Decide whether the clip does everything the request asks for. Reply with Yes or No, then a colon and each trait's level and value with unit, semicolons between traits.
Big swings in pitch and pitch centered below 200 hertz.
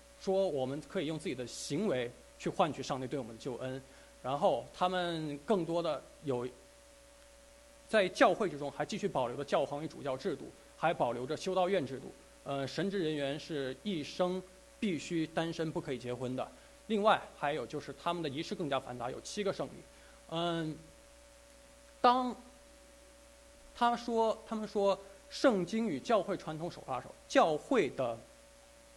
Yes: wide, 8.6 semitones; medium, 185 Hz